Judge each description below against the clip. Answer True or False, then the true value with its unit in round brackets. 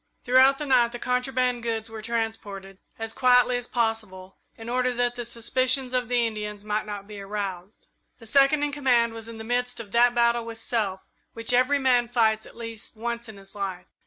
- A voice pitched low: False (235 Hz)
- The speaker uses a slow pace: False (200 wpm)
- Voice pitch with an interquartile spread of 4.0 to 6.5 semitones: False (2.4 semitones)